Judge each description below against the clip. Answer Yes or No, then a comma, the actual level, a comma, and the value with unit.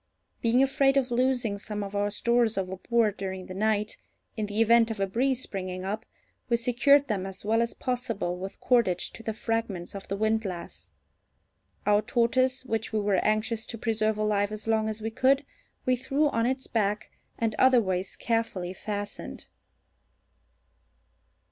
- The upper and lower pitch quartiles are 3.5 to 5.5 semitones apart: No, average, 2.9 semitones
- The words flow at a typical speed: Yes, average, 160 wpm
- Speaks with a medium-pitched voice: No, high, 220 Hz